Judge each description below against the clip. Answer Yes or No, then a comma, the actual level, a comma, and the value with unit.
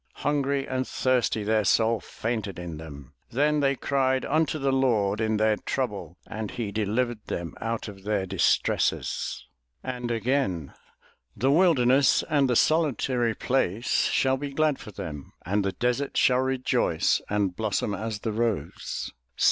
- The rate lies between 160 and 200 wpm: No, average, 150 wpm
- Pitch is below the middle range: Yes, low, 115 Hz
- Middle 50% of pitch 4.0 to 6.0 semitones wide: Yes, average, 4.4 semitones